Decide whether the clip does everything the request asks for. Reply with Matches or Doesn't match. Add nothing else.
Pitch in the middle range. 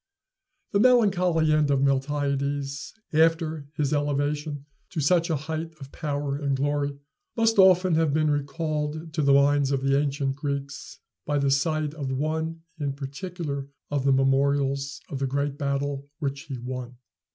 Matches